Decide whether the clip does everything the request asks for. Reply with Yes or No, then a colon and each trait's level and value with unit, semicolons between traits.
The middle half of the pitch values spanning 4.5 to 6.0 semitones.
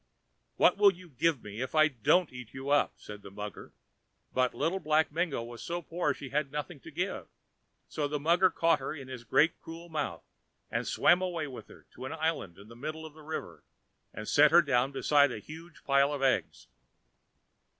No: average, 4.1 semitones